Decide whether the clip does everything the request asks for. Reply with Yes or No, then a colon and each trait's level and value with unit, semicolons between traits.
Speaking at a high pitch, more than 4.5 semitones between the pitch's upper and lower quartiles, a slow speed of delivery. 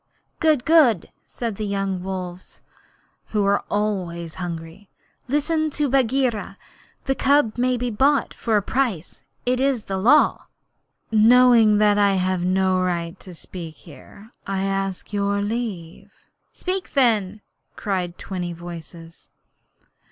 Yes: high, 200 Hz; average, 5.1 semitones; slow, 130 wpm